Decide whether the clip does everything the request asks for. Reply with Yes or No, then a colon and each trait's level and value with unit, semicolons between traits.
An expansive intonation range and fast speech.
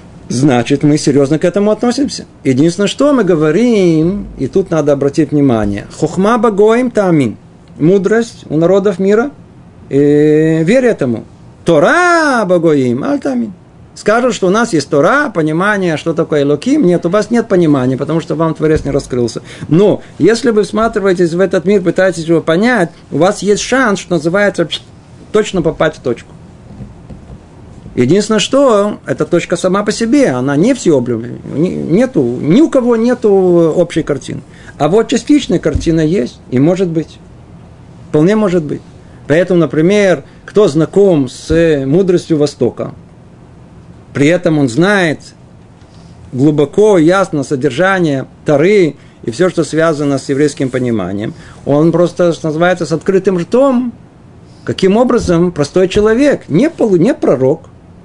No: wide, 5.7 semitones; average, 140 wpm